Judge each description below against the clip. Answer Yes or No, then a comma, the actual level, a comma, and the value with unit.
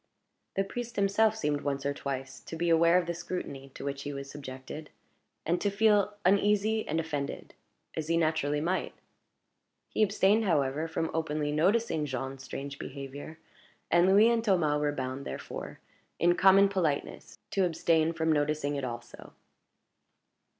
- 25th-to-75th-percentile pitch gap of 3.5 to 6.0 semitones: Yes, average, 5.2 semitones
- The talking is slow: No, average, 155 wpm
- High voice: No, medium, 160 Hz